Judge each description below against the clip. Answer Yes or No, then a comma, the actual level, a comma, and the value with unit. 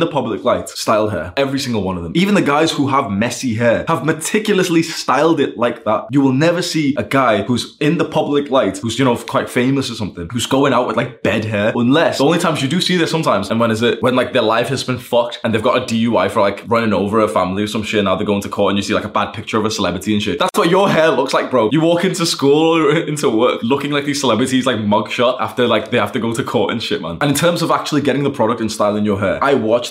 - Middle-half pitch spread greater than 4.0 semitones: Yes, average, 5.2 semitones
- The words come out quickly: Yes, fast, 290 wpm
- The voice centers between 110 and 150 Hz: Yes, low, 130 Hz